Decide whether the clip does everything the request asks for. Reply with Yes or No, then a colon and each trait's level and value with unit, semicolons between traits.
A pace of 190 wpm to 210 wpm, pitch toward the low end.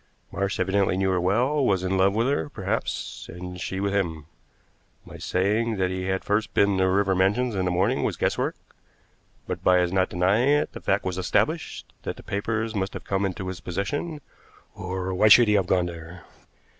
Yes: average, 200 wpm; very low, 95 Hz